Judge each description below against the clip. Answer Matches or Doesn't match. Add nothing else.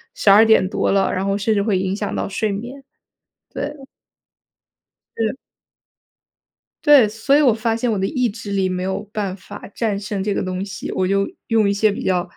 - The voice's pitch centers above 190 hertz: Matches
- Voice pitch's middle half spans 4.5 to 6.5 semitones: Doesn't match